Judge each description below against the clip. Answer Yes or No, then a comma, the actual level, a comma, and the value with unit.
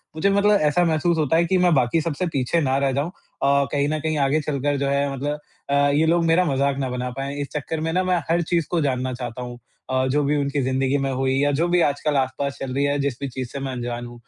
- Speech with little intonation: No, average, 3.3 semitones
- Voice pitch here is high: No, medium, 140 Hz